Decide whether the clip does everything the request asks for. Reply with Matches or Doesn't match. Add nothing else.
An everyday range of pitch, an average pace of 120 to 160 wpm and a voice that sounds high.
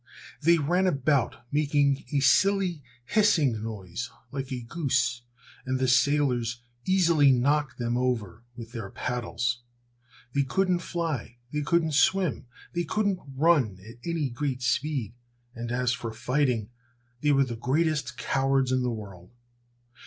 Doesn't match